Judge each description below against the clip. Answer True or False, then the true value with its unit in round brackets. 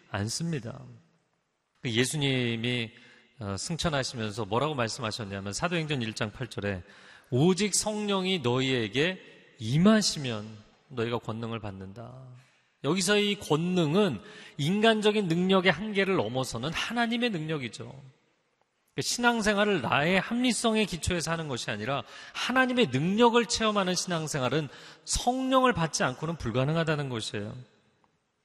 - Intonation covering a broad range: True (8.3 semitones)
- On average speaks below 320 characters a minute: True (290 characters per minute)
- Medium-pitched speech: True (150 Hz)